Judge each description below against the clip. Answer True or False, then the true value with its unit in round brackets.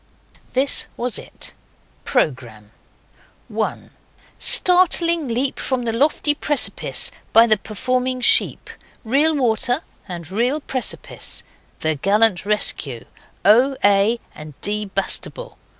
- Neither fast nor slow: False (105 wpm)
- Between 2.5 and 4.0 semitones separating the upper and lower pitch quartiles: False (5.5 semitones)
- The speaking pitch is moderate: False (235 Hz)